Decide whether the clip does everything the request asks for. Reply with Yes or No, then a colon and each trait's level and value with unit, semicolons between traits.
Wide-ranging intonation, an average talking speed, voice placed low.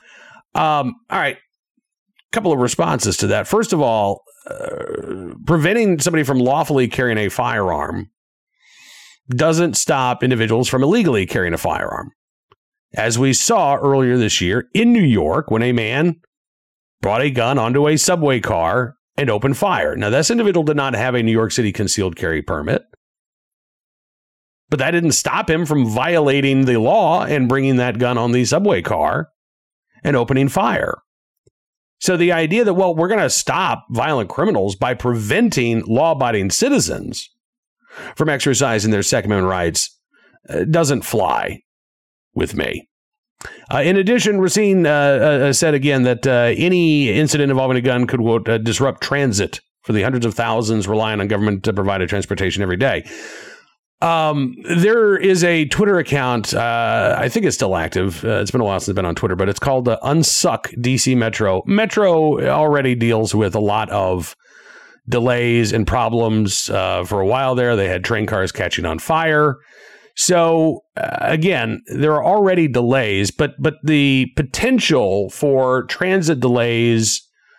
Yes: wide, 6.1 semitones; average, 160 wpm; low, 130 Hz